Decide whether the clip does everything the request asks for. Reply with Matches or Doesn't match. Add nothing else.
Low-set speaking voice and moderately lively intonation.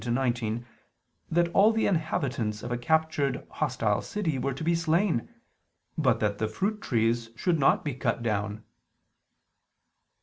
Doesn't match